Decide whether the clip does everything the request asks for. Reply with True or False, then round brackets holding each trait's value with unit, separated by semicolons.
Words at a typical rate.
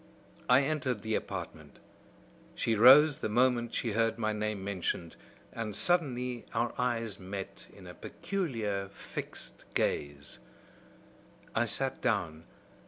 False (120 wpm)